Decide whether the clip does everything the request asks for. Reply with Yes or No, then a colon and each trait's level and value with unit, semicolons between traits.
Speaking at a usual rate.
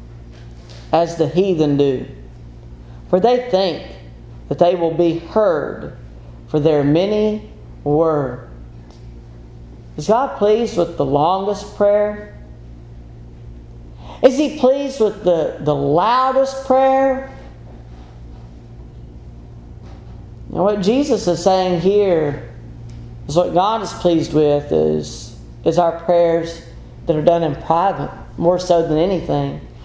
No: slow, 115 wpm